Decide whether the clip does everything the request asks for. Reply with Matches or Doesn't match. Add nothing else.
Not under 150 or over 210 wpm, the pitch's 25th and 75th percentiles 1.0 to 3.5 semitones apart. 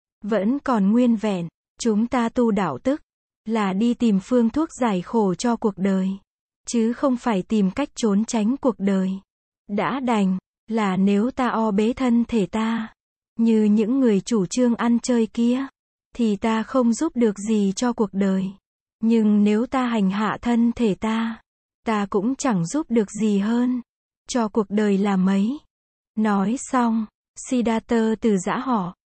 Matches